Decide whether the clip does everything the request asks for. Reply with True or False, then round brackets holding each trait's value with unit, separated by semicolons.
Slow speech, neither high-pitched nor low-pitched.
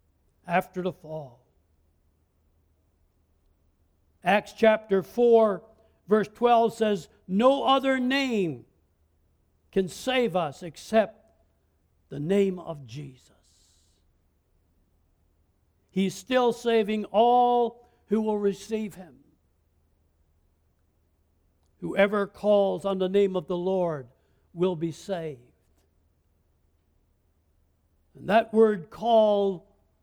True (85 wpm; 145 Hz)